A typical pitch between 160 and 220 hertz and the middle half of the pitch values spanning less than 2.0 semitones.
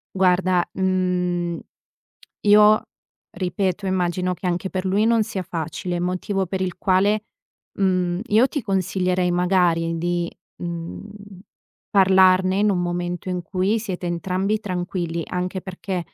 Yes: medium, 185 Hz; narrow, 1.4 semitones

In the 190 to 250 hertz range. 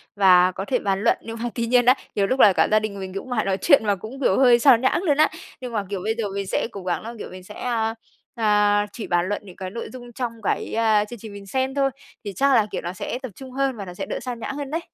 Yes: high, 225 Hz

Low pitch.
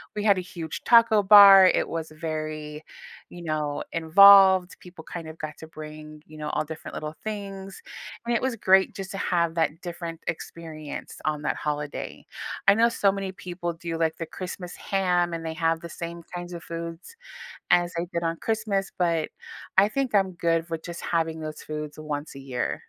No: medium, 170 Hz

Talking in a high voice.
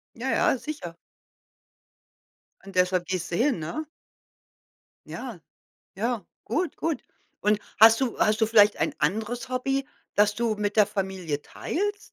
Yes: high, 215 Hz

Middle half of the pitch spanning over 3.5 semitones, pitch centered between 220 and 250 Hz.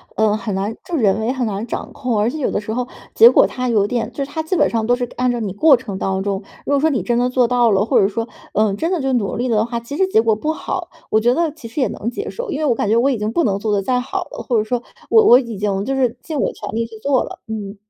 Yes: average, 4.0 semitones; high, 235 Hz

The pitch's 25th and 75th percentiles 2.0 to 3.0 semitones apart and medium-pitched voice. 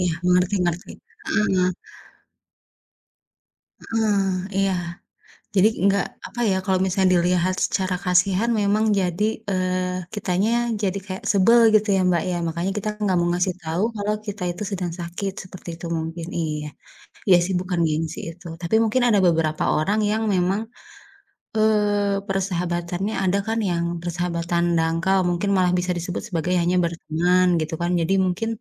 Yes: narrow, 2.4 semitones; medium, 180 Hz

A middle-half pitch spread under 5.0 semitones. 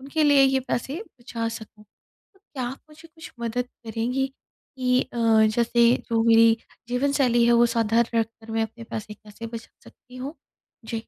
Yes: average, 2.7 semitones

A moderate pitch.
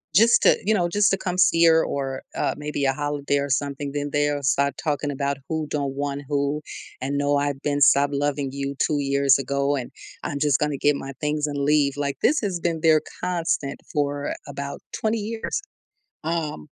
Yes: medium, 145 Hz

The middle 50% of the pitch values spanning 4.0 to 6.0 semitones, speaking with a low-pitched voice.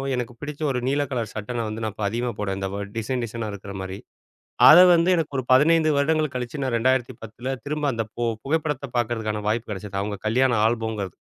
Yes: average, 4.5 semitones; low, 120 Hz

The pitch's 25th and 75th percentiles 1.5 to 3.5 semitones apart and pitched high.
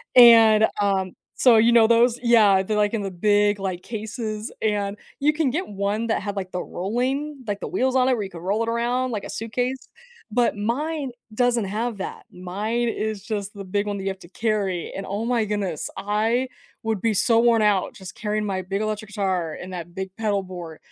Yes: average, 3.1 semitones; high, 215 Hz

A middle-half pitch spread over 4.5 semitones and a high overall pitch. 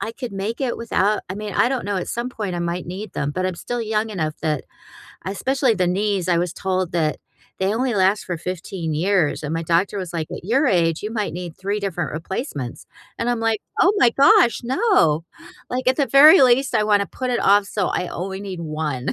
Yes: average, 5.1 semitones; high, 195 Hz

